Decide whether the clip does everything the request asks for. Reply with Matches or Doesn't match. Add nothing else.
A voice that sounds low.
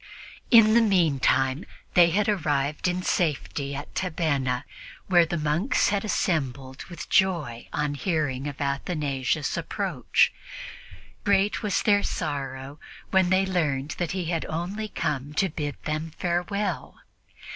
Doesn't match